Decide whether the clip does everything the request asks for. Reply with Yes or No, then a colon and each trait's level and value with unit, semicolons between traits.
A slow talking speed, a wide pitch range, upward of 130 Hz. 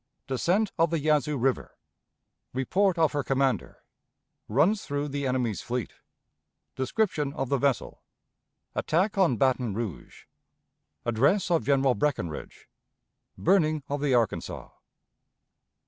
No: slow, 115 wpm; average, 4.2 semitones; medium, 140 Hz